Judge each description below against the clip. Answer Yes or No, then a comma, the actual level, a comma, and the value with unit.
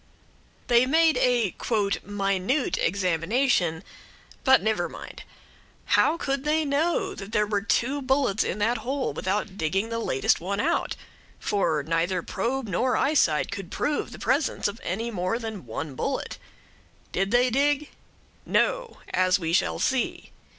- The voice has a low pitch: No, high, 220 Hz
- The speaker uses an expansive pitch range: Yes, wide, 6.2 semitones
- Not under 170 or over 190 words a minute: No, average, 145 wpm